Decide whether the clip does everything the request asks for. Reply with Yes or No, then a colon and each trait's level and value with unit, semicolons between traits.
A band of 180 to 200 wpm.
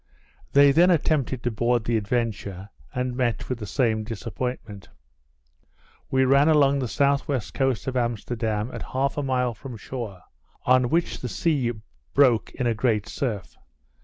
No: average, 155 wpm